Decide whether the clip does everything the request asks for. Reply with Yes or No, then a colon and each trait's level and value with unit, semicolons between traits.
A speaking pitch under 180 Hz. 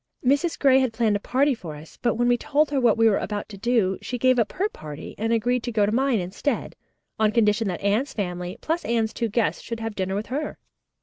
No: high, 225 Hz